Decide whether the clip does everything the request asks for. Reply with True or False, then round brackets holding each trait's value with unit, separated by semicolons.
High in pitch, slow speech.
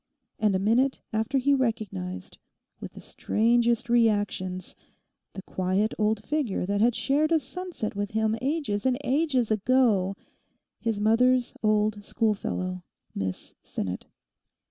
True (220 Hz; 120 wpm)